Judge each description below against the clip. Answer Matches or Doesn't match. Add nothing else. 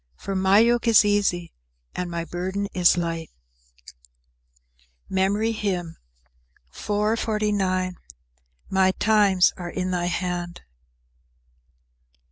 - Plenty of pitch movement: Doesn't match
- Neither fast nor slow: Doesn't match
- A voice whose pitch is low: Doesn't match